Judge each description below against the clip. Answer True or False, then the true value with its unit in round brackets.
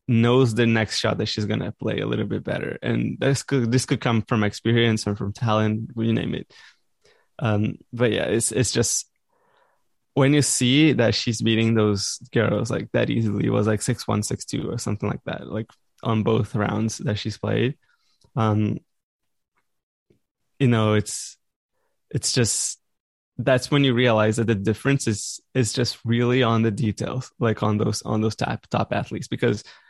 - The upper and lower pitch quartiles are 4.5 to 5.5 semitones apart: False (2.7 semitones)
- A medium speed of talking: True (185 wpm)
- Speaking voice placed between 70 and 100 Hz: False (115 Hz)